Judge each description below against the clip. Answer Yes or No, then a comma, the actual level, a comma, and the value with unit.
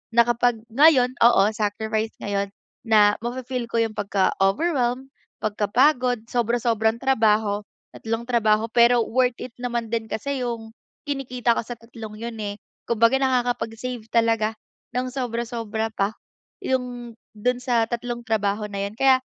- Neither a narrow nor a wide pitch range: No, narrow, 2.1 semitones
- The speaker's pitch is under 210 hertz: No, high, 235 Hz